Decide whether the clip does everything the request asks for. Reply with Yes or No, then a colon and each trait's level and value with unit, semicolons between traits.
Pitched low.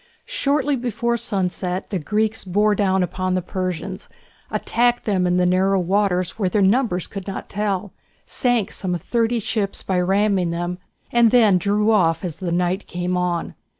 No: high, 195 Hz